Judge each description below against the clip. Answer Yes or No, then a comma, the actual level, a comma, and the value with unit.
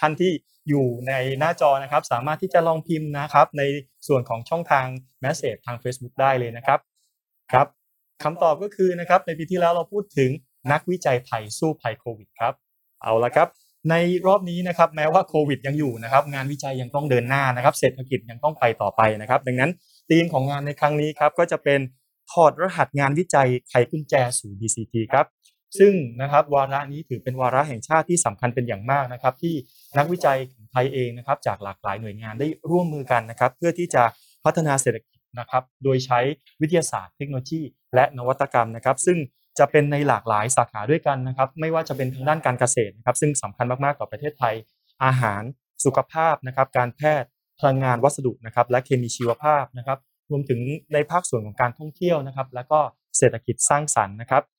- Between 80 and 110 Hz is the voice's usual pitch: No, low, 135 Hz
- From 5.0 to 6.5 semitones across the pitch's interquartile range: No, average, 3.7 semitones